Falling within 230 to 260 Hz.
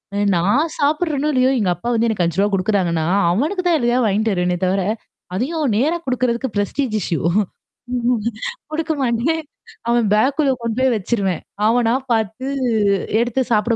Yes: high, 235 Hz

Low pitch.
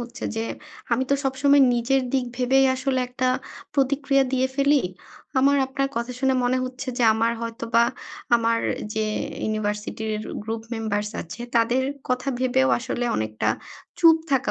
No: very high, 250 Hz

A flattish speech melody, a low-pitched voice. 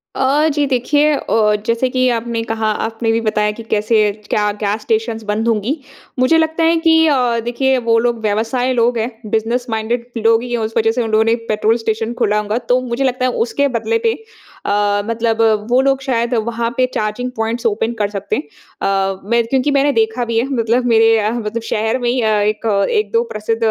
No: narrow, 2.3 semitones; high, 230 Hz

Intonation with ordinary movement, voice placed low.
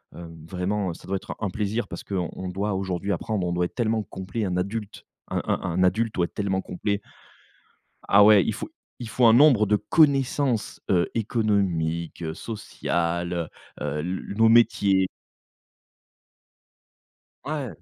Yes: average, 3.7 semitones; low, 100 Hz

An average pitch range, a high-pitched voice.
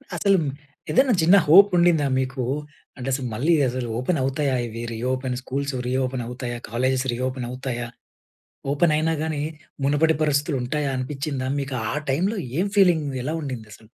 No: average, 3.6 semitones; low, 135 Hz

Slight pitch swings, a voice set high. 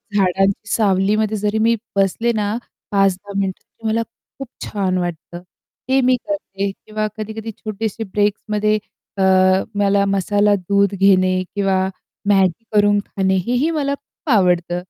Yes: narrow, 2.0 semitones; high, 205 Hz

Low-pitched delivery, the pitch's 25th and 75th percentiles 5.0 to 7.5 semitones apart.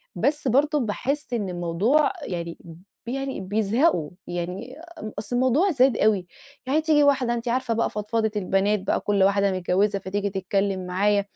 No: high, 210 Hz; wide, 5.4 semitones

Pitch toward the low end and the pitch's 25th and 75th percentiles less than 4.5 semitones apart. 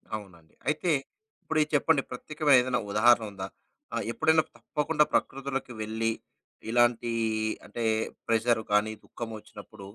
No: low, 120 Hz; average, 5.1 semitones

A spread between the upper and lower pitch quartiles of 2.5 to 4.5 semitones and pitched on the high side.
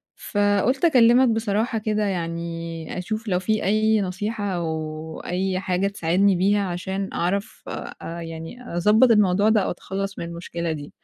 Yes: average, 3.9 semitones; high, 195 Hz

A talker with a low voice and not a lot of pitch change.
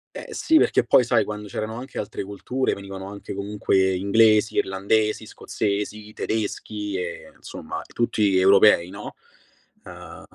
Yes: low, 105 Hz; narrow, 1.8 semitones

